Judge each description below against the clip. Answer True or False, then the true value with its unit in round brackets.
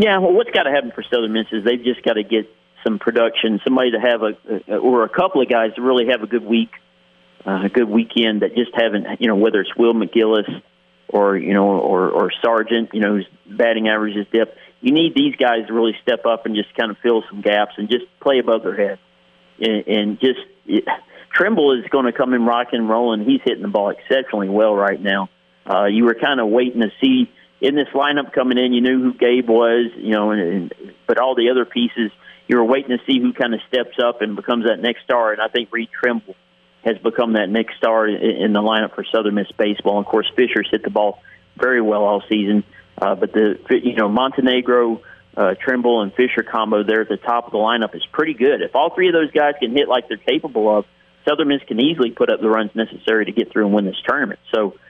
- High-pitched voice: False (115 Hz)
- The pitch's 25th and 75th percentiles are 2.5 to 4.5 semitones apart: True (2.9 semitones)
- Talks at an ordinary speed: False (235 wpm)